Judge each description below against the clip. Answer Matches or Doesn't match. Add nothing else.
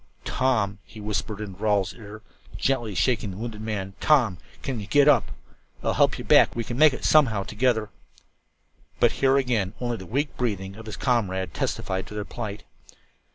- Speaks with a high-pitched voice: Doesn't match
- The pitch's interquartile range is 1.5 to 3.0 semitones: Doesn't match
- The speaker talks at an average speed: Matches